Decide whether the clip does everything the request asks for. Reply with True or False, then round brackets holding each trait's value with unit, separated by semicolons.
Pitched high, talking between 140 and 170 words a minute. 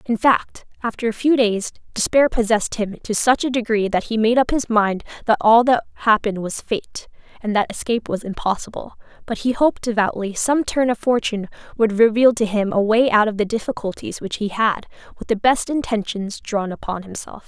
False (220 Hz; 200 wpm)